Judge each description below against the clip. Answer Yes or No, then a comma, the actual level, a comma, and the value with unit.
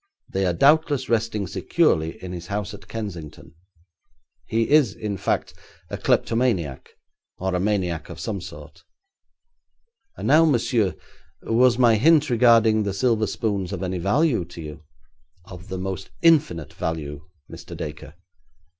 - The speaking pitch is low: Yes, low, 100 Hz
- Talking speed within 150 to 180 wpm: No, average, 140 wpm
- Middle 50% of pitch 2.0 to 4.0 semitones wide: No, average, 5.0 semitones